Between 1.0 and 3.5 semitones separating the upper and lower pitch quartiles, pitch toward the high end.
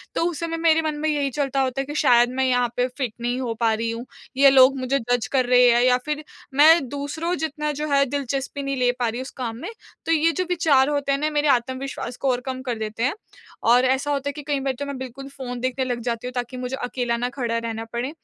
Yes: narrow, 2.5 semitones; very high, 260 Hz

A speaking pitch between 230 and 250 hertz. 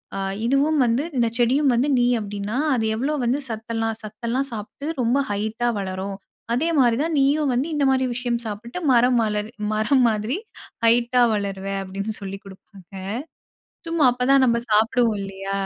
Yes: high, 235 Hz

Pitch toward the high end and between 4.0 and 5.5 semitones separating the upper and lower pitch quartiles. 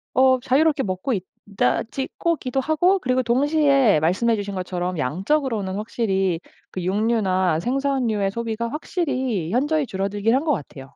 No: high, 230 Hz; wide, 6.1 semitones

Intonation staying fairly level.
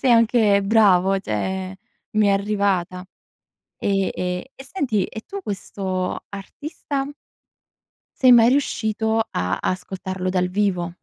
No: average, 3.2 semitones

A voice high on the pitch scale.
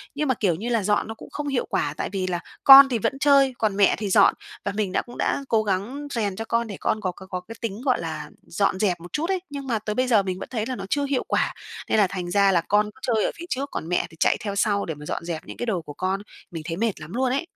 Yes: high, 210 Hz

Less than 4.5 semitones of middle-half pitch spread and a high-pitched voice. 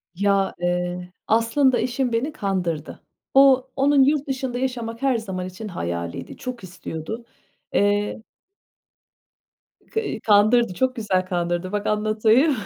No: wide, 5.6 semitones; high, 215 Hz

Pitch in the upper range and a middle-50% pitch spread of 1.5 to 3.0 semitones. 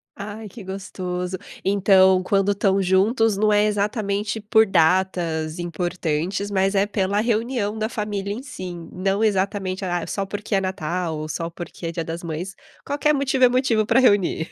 Yes: high, 195 Hz; average, 2.7 semitones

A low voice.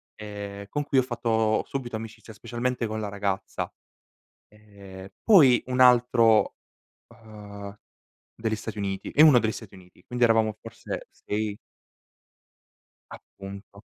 Yes: low, 110 Hz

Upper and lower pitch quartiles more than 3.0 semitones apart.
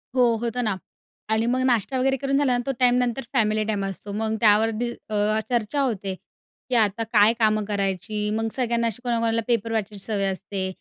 No: narrow, 2.6 semitones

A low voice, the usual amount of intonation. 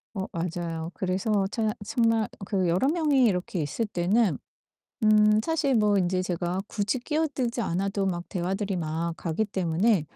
No: high, 195 Hz; average, 4.3 semitones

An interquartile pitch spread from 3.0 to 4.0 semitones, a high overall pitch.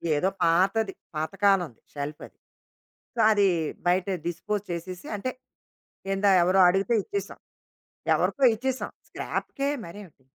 Yes: average, 3.4 semitones; high, 195 Hz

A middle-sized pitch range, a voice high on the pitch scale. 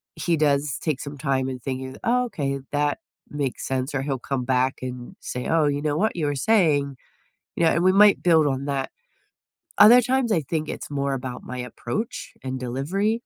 No: average, 4.1 semitones; medium, 145 Hz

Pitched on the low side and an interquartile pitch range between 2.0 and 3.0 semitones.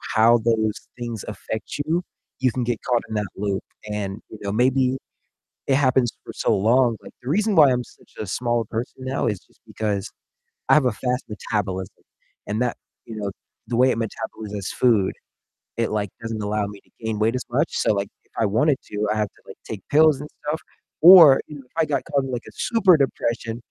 No: low, 115 Hz; average, 3.7 semitones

